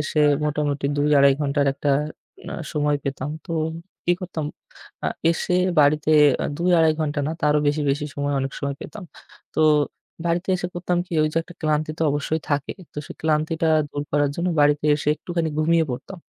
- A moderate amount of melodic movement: No, narrow, 2.3 semitones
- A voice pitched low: No, medium, 150 Hz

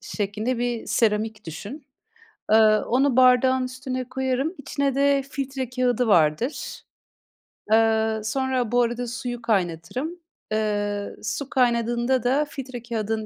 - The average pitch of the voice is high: Yes, high, 245 Hz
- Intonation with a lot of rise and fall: No, average, 3.0 semitones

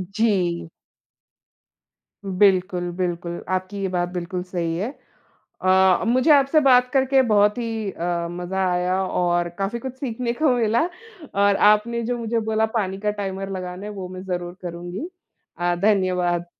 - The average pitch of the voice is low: No, high, 190 Hz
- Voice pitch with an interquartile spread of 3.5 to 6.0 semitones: Yes, average, 3.9 semitones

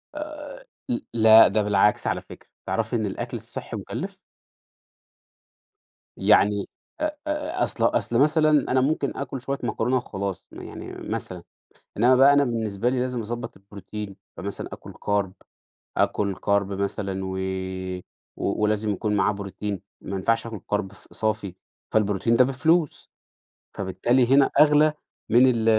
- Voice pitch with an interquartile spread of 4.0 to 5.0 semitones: Yes, average, 4.6 semitones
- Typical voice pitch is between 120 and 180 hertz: No, low, 110 Hz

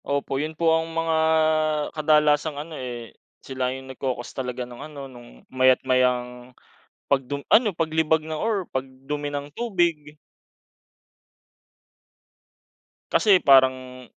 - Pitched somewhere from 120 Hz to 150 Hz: Yes, medium, 140 Hz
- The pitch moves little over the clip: No, average, 3.5 semitones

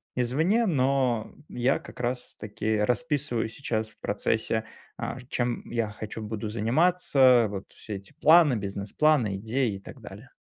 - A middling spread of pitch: Yes, average, 4.2 semitones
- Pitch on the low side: Yes, low, 120 Hz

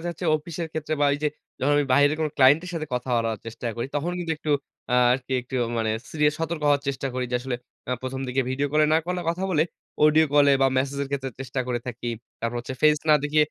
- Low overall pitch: No, medium, 145 Hz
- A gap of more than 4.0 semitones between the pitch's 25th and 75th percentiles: No, average, 3.0 semitones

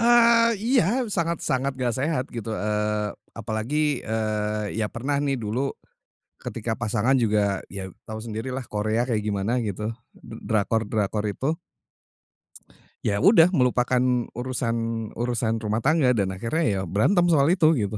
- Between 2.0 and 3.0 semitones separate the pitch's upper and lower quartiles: No, average, 4.6 semitones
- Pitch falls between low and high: No, low, 115 Hz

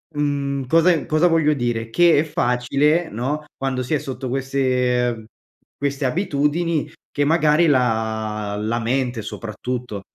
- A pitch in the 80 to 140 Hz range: Yes, low, 135 Hz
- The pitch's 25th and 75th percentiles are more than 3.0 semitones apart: Yes, average, 3.7 semitones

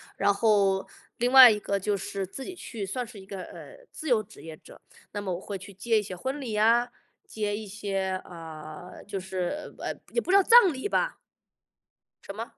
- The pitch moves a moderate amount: Yes, average, 4.4 semitones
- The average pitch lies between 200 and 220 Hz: Yes, high, 205 Hz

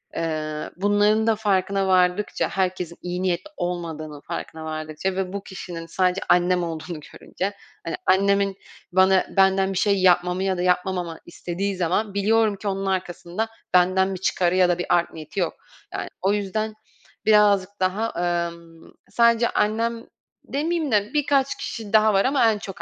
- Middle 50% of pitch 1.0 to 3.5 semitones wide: Yes, average, 2.7 semitones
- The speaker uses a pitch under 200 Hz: Yes, high, 190 Hz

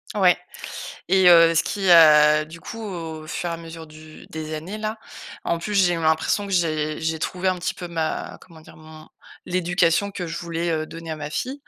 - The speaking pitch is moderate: Yes, medium, 165 Hz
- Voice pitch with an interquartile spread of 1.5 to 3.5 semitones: Yes, narrow, 2.5 semitones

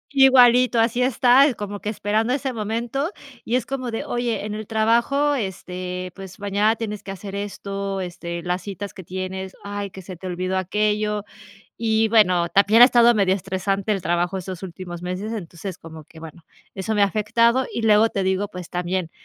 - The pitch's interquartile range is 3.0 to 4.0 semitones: Yes, average, 3.4 semitones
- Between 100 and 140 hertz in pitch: No, high, 205 Hz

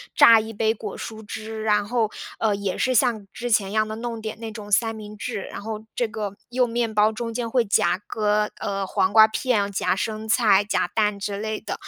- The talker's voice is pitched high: Yes, high, 215 Hz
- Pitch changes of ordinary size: No, narrow, 1.4 semitones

